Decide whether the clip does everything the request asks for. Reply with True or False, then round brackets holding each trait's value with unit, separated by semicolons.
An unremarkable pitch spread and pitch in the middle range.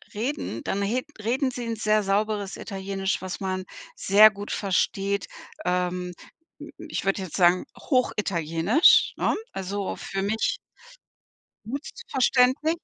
False (3.2 semitones; 200 Hz)